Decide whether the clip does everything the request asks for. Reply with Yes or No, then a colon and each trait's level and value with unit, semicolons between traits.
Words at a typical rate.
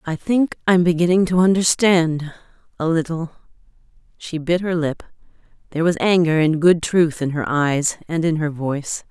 Yes: average, 160 wpm